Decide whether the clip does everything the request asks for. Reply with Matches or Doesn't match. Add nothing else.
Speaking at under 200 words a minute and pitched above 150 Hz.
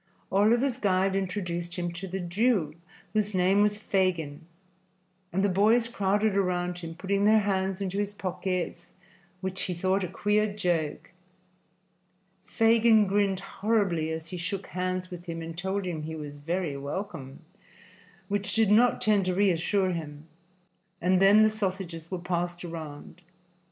Matches